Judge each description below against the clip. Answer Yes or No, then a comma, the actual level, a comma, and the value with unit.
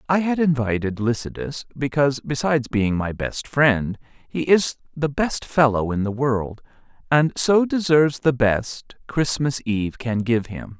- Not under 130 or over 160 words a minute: Yes, average, 155 wpm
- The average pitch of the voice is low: Yes, low, 130 Hz